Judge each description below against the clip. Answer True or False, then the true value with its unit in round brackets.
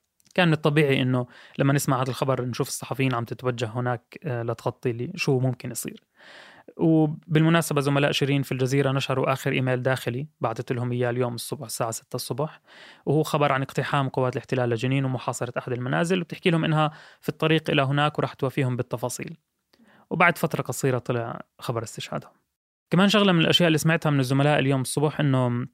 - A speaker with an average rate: False (170 wpm)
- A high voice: False (135 Hz)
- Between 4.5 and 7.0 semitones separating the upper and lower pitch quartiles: False (3.5 semitones)